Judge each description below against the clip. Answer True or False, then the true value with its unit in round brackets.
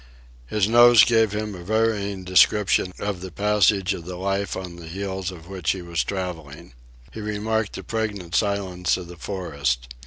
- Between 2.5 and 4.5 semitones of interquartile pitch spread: True (2.9 semitones)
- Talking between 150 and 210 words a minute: True (175 wpm)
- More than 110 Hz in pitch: False (95 Hz)